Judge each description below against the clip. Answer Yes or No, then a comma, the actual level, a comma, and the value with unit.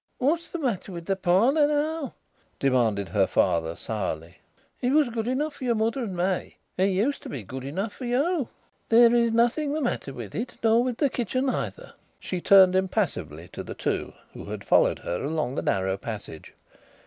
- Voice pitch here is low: No, high, 215 Hz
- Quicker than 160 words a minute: Yes, average, 190 wpm